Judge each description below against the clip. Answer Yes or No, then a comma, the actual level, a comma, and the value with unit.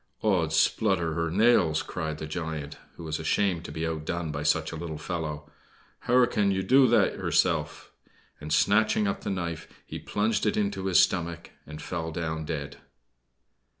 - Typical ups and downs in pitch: Yes, average, 4.0 semitones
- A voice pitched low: Yes, very low, 85 Hz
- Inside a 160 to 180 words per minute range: Yes, average, 165 wpm